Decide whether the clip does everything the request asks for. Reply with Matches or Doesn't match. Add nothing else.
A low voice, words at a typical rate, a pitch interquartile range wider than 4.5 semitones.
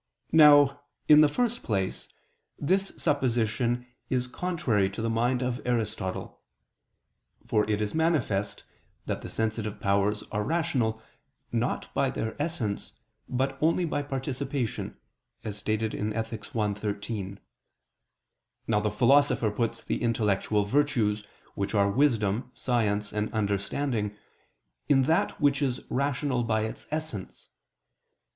Doesn't match